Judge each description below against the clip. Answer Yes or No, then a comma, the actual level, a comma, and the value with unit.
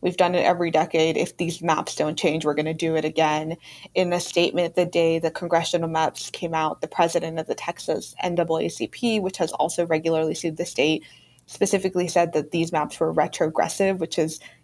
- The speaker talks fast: No, average, 195 wpm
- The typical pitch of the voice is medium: Yes, medium, 165 Hz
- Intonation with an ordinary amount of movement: No, narrow, 1.7 semitones